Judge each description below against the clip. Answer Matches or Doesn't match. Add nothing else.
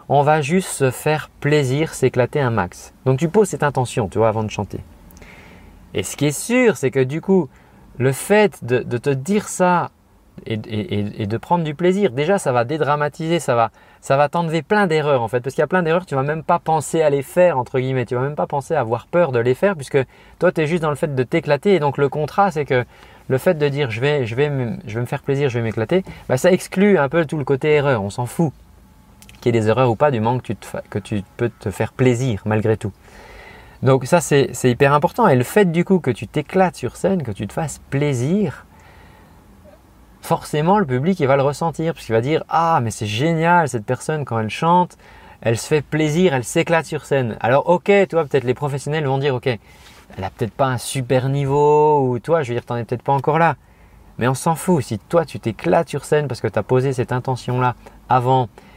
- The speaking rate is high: Matches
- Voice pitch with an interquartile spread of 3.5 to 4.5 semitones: Doesn't match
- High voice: Doesn't match